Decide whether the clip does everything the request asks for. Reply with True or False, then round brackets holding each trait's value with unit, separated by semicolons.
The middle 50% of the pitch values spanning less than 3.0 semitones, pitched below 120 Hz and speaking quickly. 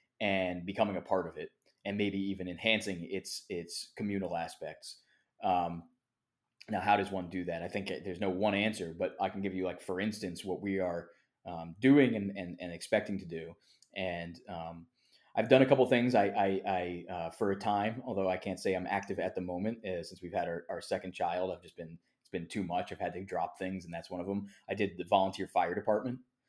True (2.5 semitones; 95 Hz; 230 wpm)